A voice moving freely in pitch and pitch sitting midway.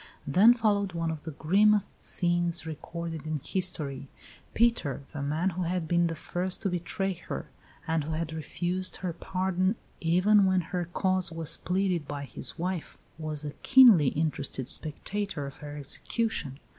No: average, 3.3 semitones; medium, 170 Hz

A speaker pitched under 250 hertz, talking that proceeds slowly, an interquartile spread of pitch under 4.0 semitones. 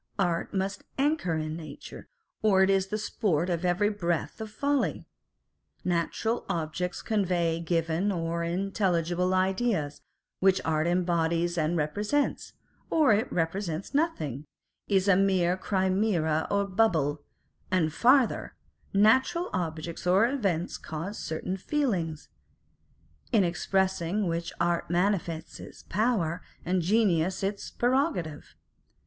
Yes: medium, 185 Hz; slow, 120 wpm; average, 3.6 semitones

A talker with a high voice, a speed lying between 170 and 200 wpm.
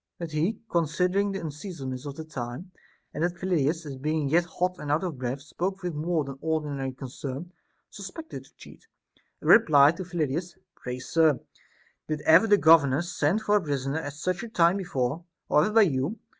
No: medium, 160 Hz; average, 190 wpm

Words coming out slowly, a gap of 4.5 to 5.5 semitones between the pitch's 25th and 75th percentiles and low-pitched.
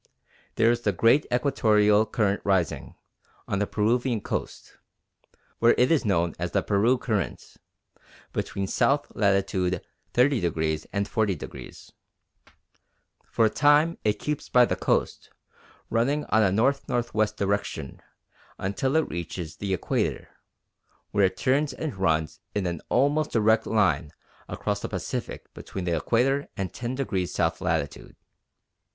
Yes: slow, 130 wpm; average, 4.9 semitones; low, 105 Hz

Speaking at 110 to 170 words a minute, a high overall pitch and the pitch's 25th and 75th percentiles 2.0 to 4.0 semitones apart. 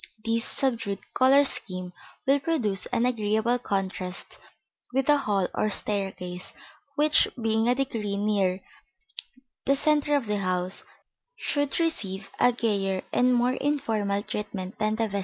No: average, 140 wpm; high, 220 Hz; average, 4.8 semitones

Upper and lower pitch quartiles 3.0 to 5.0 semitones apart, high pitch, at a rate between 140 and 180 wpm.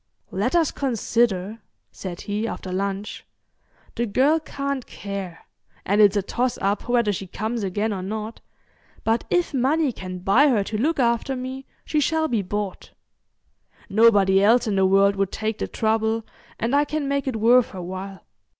Yes: average, 4.5 semitones; high, 220 Hz; average, 170 wpm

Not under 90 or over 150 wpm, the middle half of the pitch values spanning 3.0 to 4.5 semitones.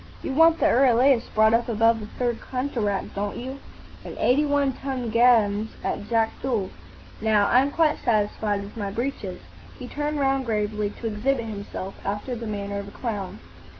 No: average, 170 wpm; average, 4.1 semitones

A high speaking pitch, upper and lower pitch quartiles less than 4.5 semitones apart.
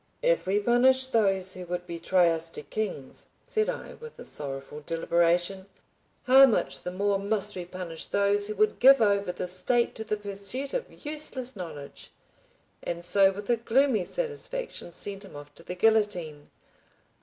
No: high, 200 Hz; average, 5.1 semitones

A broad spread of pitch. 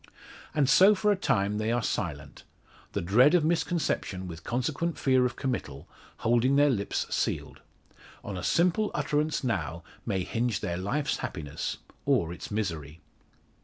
Yes: wide, 8.1 semitones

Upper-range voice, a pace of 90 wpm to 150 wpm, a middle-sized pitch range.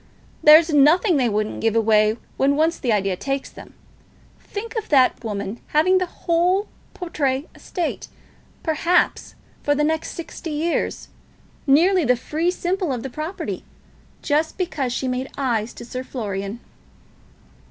No: very high, 290 Hz; average, 140 wpm; wide, 5.9 semitones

